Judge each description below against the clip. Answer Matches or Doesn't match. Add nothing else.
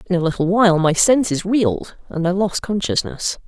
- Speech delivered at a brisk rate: Doesn't match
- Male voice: Doesn't match